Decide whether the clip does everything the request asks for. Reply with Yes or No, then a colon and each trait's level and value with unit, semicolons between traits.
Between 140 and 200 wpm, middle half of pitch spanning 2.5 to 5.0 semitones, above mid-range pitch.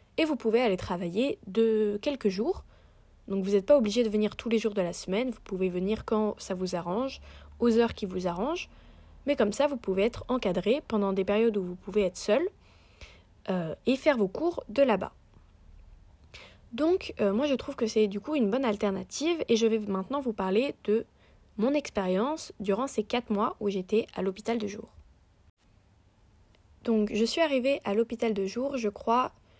Yes: average, 195 wpm; average, 4.2 semitones; high, 215 Hz